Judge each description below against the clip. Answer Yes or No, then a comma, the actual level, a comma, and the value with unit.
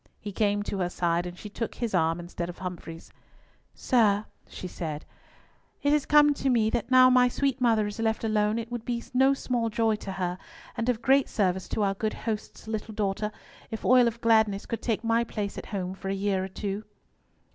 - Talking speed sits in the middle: No, fast, 210 wpm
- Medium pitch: No, high, 215 Hz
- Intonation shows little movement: No, average, 3.5 semitones